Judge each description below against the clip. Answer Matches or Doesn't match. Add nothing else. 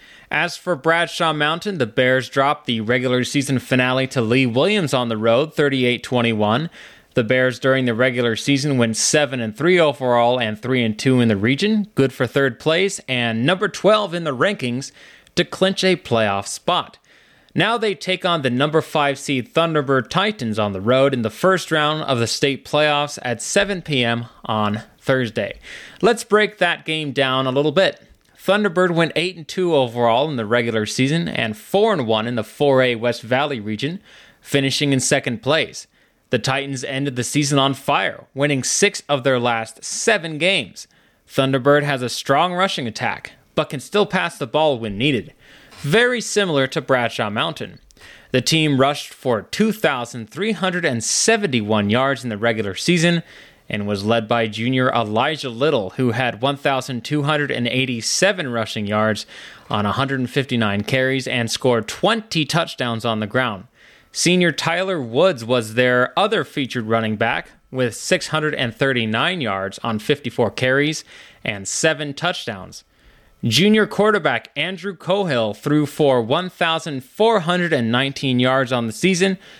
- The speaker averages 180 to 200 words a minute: Doesn't match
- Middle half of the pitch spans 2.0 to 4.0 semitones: Doesn't match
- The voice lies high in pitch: Doesn't match